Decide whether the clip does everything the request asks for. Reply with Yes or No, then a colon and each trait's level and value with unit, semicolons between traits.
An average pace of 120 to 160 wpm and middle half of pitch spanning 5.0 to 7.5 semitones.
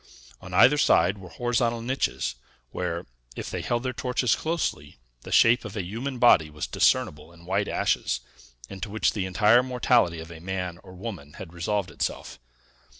No: average, 170 wpm; wide, 5.6 semitones